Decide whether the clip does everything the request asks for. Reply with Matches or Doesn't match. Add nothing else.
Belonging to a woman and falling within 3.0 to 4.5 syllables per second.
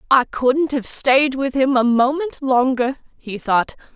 Matches